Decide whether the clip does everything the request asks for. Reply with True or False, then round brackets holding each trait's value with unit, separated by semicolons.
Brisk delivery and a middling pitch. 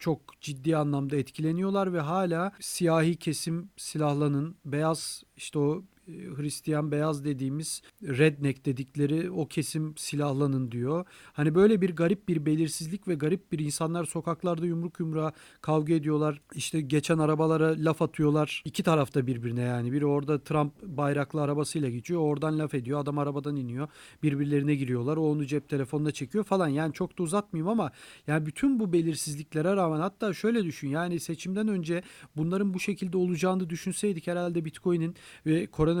True (150 wpm; 155 Hz)